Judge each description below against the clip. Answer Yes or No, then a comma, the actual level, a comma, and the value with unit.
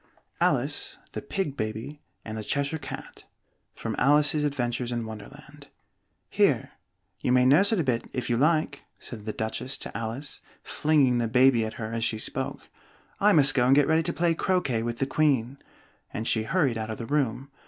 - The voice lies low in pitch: Yes, low, 130 Hz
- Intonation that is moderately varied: Yes, average, 4.4 semitones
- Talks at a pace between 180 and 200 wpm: Yes, average, 185 wpm